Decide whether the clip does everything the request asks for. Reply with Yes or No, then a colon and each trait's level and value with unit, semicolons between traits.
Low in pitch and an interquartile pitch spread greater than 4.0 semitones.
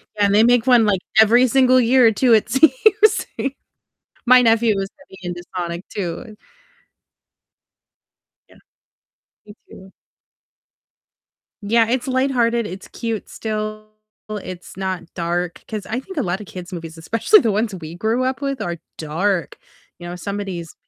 No: high, 215 Hz; average, 4.8 semitones